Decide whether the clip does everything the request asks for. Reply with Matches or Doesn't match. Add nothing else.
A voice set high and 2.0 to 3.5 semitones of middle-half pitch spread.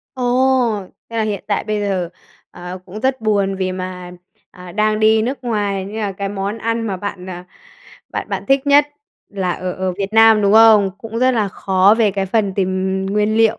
Matches